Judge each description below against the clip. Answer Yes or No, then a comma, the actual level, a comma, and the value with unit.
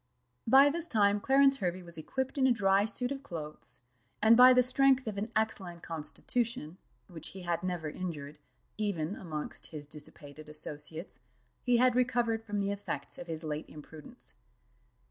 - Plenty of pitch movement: Yes, wide, 7.6 semitones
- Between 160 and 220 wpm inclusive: Yes, average, 165 wpm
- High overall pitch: Yes, high, 195 Hz